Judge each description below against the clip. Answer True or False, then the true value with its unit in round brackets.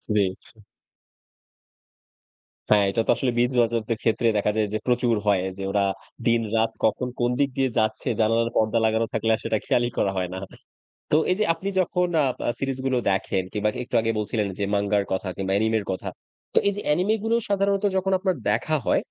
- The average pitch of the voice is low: True (115 Hz)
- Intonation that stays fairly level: False (4.3 semitones)